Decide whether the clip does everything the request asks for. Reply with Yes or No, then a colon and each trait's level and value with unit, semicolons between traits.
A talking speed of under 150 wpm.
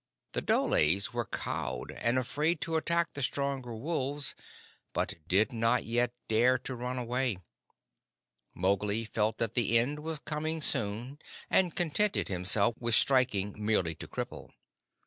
Yes: average, 140 wpm